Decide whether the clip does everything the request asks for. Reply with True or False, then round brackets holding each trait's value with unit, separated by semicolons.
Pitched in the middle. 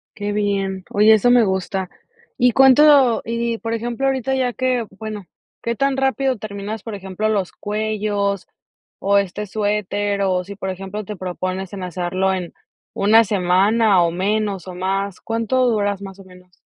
False (205 Hz)